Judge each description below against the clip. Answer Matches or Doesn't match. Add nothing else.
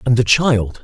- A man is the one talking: Matches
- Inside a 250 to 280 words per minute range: Doesn't match